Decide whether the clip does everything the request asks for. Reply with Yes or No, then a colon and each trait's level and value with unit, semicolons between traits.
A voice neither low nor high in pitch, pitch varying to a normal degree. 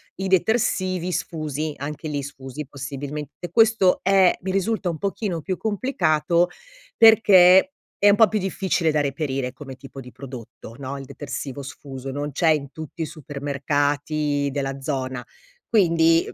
Yes: medium, 150 Hz; average, 5.0 semitones